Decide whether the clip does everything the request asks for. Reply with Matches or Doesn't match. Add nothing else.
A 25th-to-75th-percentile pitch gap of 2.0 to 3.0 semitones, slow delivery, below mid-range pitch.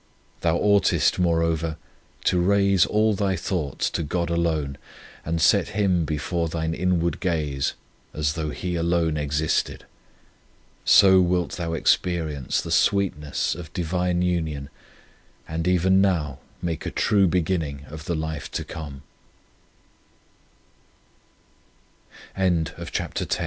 Matches